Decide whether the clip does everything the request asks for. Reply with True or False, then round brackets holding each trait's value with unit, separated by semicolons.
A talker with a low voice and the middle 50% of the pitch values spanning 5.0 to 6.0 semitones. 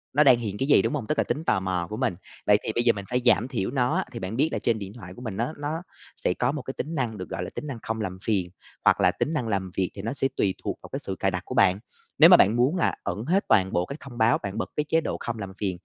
True (115 Hz; 5.5 semitones)